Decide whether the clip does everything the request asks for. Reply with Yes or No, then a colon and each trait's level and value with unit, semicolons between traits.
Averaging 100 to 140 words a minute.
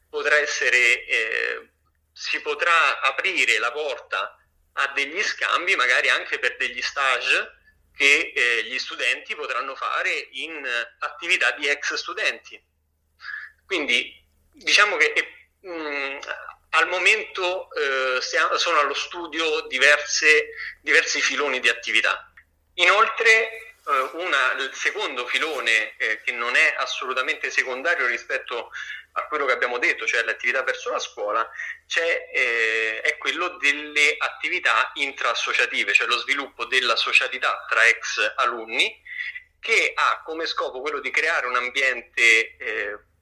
Yes: average, 130 wpm